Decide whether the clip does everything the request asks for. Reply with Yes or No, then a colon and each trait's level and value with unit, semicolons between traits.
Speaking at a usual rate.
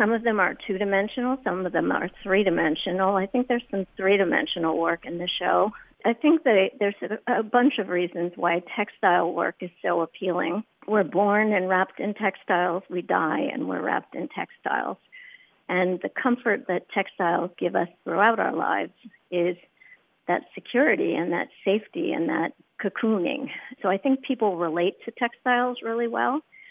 Yes: average, 175 wpm